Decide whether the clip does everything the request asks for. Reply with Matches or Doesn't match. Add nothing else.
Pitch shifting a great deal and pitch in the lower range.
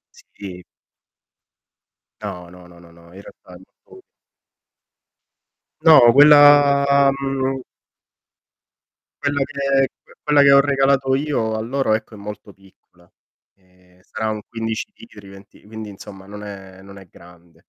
Matches